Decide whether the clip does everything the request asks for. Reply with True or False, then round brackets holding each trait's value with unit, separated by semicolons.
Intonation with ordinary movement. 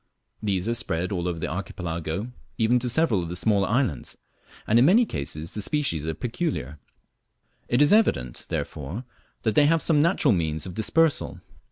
False (8.8 semitones)